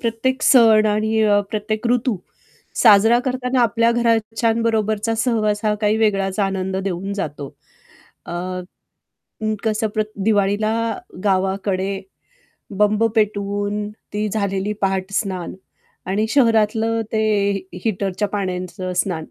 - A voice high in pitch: Yes, high, 210 Hz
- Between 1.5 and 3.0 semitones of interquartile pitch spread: Yes, narrow, 2.4 semitones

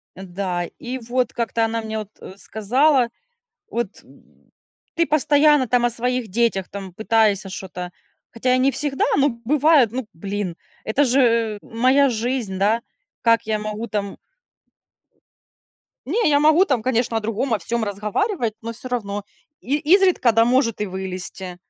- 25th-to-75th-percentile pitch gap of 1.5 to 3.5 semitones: No, average, 3.9 semitones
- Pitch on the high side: Yes, high, 230 Hz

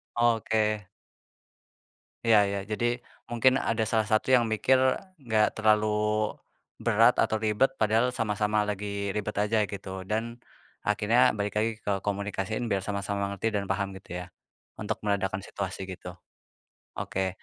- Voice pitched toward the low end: Yes, low, 105 Hz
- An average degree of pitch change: No, narrow, 2.0 semitones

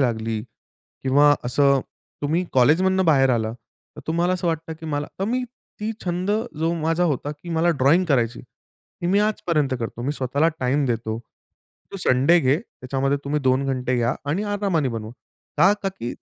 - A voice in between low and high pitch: Yes, medium, 145 Hz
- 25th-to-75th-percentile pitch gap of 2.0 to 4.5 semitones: No, average, 5.1 semitones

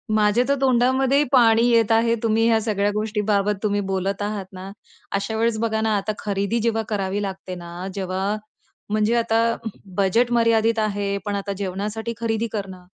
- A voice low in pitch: No, high, 215 Hz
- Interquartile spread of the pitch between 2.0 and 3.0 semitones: Yes, narrow, 2.4 semitones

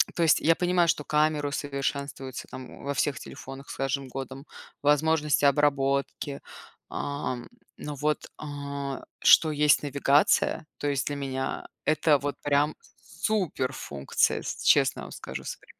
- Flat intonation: Yes, narrow, 1.6 semitones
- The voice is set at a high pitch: No, medium, 145 Hz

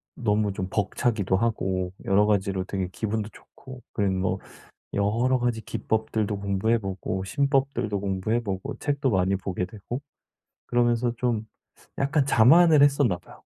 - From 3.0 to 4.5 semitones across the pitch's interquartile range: Yes, average, 3.9 semitones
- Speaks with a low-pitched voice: Yes, low, 110 Hz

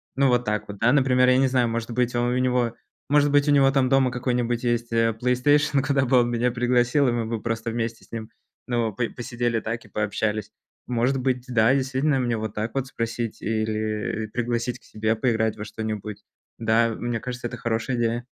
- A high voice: No, low, 120 Hz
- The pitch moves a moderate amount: No, narrow, 2.1 semitones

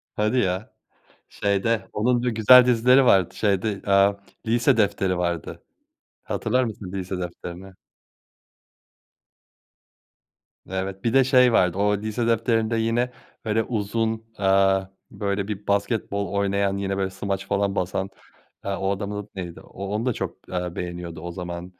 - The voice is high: No, low, 100 Hz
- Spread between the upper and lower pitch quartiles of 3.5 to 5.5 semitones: No, average, 2.8 semitones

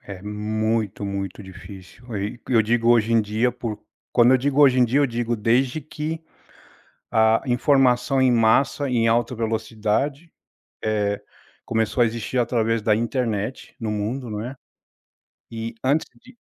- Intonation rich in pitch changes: No, average, 2.7 semitones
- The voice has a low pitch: Yes, low, 115 Hz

